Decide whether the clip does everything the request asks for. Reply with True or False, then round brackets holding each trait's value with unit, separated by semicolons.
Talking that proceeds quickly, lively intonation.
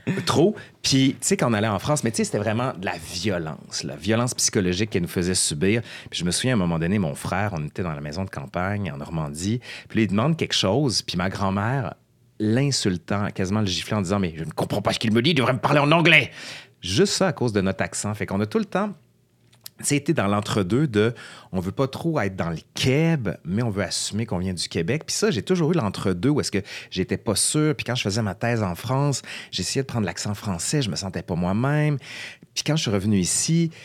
True (250 wpm; 6.2 semitones)